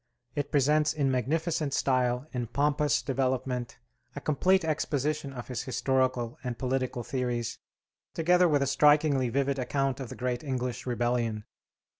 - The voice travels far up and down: No, average, 2.8 semitones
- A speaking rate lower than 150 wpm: Yes, average, 140 wpm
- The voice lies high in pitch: No, low, 130 Hz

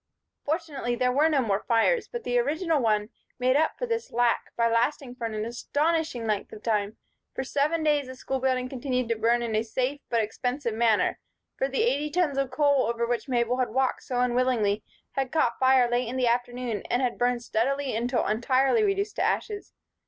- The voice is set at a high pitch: Yes, very high, 250 Hz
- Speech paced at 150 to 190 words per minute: No, average, 200 wpm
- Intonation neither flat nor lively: Yes, average, 3.4 semitones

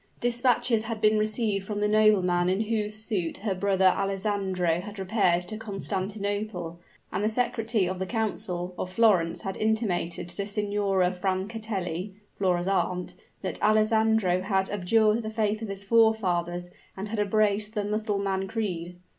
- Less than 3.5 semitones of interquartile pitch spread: Yes, average, 2.7 semitones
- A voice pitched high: Yes, high, 200 Hz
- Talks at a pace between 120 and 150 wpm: Yes, average, 145 wpm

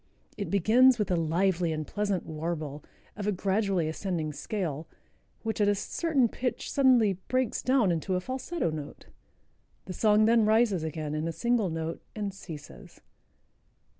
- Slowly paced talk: No, average, 155 wpm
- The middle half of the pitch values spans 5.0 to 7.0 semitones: Yes, wide, 5.4 semitones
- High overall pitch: Yes, high, 195 Hz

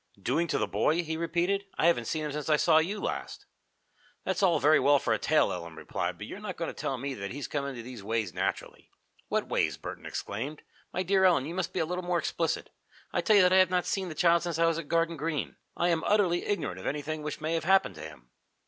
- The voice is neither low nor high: Yes, medium, 160 Hz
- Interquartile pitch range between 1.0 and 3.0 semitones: No, average, 4.0 semitones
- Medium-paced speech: No, fast, 255 wpm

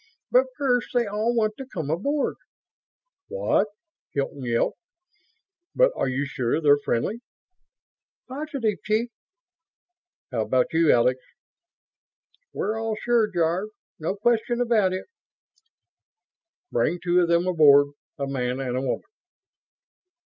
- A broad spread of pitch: Yes, wide, 8.7 semitones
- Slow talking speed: Yes, slow, 120 wpm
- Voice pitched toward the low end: No, medium, 185 Hz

